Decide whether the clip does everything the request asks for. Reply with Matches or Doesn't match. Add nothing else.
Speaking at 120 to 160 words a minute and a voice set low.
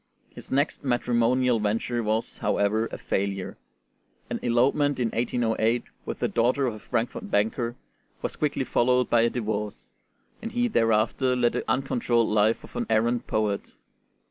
Matches